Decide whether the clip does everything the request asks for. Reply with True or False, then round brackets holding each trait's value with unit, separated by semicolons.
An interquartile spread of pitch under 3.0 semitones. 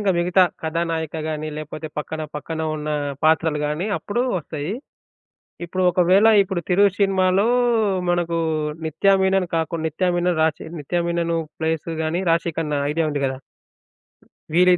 True (2.5 semitones)